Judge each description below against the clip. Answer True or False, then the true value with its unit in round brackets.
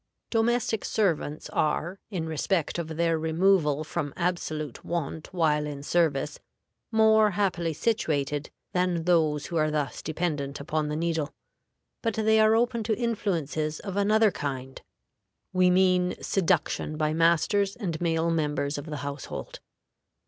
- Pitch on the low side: False (165 Hz)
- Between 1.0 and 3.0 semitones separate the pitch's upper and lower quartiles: False (4.3 semitones)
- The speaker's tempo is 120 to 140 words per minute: True (135 wpm)